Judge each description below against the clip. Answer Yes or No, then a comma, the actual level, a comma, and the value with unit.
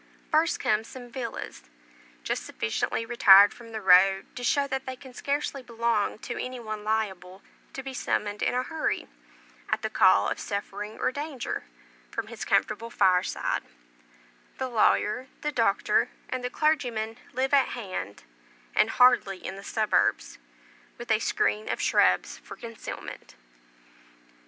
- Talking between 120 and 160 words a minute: Yes, average, 145 wpm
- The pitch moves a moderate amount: Yes, average, 3.8 semitones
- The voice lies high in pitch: Yes, high, 230 Hz